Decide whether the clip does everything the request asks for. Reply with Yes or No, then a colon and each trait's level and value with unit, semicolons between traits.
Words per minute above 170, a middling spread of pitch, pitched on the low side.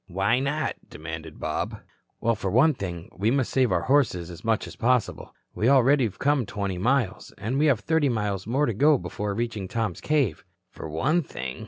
No: average, 195 wpm; wide, 6.0 semitones; low, 115 Hz